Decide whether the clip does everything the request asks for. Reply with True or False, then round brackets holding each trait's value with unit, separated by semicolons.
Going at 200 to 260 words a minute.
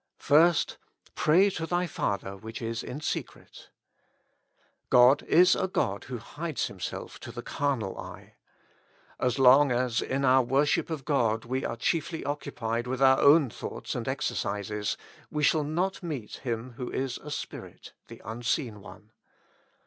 False (150 wpm)